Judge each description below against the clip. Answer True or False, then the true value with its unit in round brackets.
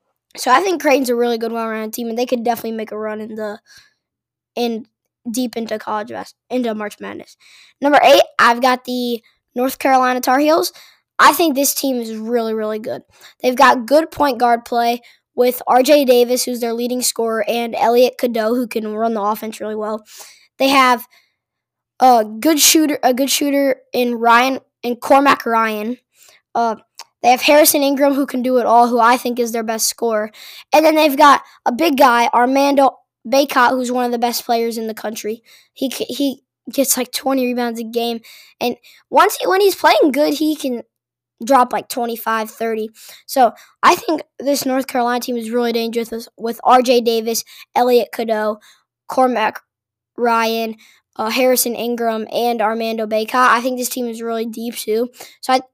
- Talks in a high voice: True (245 Hz)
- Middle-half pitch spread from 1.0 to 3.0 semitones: True (2.6 semitones)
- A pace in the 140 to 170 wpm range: False (180 wpm)